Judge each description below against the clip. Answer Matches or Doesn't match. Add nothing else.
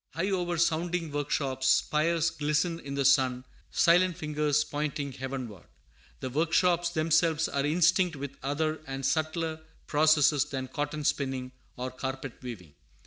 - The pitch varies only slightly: Doesn't match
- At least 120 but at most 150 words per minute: Matches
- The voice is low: Doesn't match